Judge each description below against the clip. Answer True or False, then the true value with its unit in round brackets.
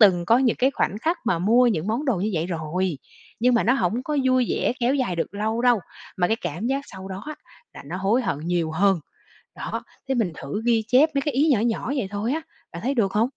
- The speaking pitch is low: False (220 Hz)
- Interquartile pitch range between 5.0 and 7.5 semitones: True (5.4 semitones)